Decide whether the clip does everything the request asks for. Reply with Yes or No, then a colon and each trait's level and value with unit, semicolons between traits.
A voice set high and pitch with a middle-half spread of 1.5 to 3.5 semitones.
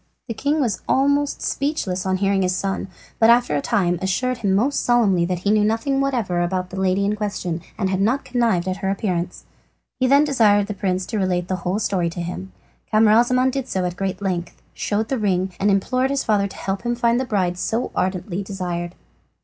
No: high, 200 Hz; average, 4.4 semitones